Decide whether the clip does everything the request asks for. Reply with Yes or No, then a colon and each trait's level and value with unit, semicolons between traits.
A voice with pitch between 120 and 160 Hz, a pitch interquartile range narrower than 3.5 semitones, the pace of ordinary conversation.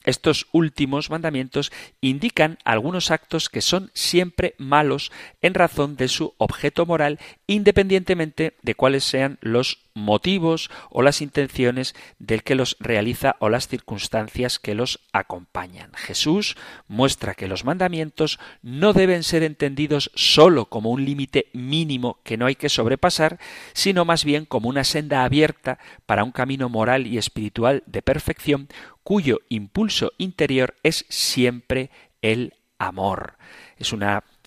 No: medium, 140 Hz; average, 4.6 semitones; average, 135 wpm